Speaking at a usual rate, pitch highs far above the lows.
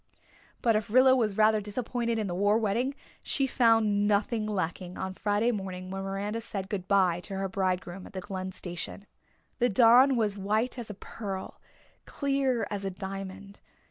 No: average, 175 wpm; average, 3.1 semitones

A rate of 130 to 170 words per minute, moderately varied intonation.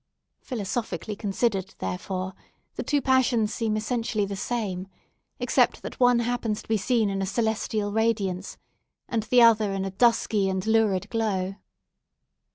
Yes: average, 145 wpm; average, 3.1 semitones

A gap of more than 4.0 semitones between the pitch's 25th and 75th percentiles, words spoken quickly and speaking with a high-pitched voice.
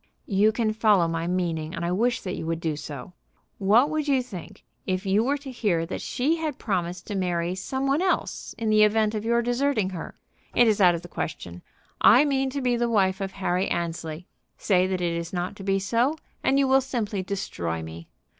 Yes: wide, 5.6 semitones; fast, 220 wpm; high, 195 Hz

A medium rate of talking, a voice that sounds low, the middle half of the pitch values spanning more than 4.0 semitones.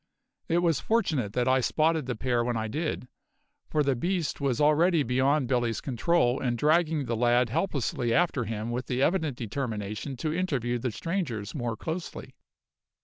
Yes: average, 165 wpm; low, 130 Hz; average, 5.0 semitones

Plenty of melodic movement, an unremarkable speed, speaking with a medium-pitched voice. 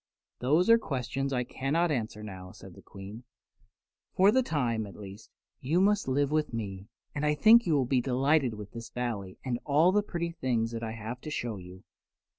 No: wide, 5.7 semitones; average, 195 wpm; low, 125 Hz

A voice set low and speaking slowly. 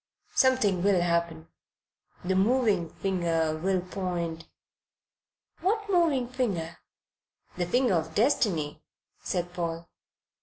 No: medium, 180 Hz; slow, 105 wpm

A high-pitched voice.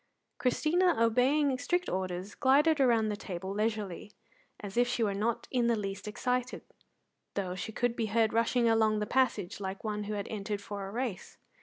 Yes: high, 220 Hz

